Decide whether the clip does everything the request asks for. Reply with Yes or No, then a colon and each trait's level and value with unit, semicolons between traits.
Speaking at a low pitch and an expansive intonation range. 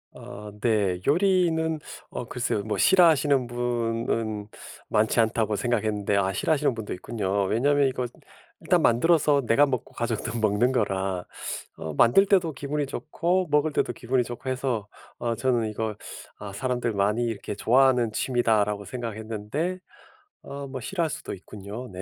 No: low, 120 Hz; average, 4.7 semitones